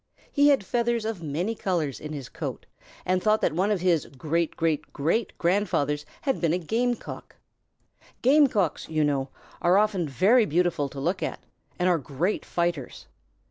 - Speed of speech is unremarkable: Yes, average, 175 wpm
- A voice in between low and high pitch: Yes, medium, 175 Hz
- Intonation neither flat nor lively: No, wide, 5.8 semitones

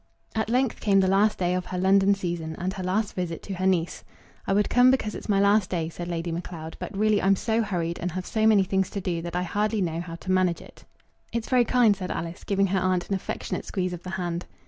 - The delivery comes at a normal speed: No, fast, 255 wpm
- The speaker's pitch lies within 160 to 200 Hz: Yes, high, 190 Hz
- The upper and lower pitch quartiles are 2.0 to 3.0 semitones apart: Yes, average, 2.7 semitones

